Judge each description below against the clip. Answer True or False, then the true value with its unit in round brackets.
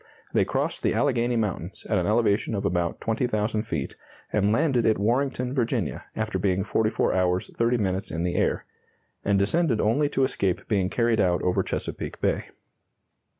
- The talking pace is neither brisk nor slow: True (165 wpm)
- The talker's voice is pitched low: True (110 Hz)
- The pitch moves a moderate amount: True (4.0 semitones)